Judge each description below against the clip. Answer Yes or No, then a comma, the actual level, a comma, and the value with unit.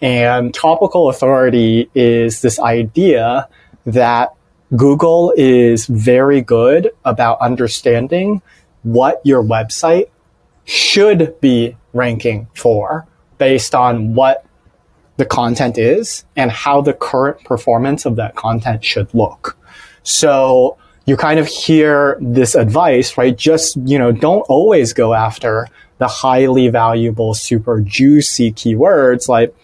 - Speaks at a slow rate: Yes, slow, 115 wpm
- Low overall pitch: Yes, low, 125 Hz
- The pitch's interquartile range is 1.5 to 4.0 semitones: Yes, average, 3.3 semitones